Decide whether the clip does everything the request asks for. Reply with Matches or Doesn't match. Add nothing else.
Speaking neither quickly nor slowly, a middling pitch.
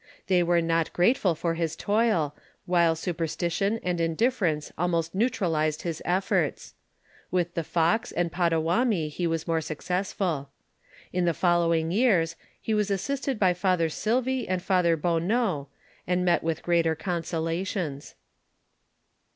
Doesn't match